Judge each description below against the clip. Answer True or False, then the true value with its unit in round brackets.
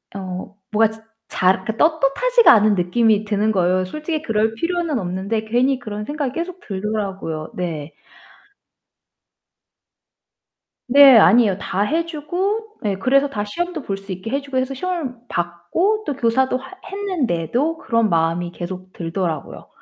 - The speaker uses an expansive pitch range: True (7.6 semitones)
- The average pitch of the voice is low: False (225 Hz)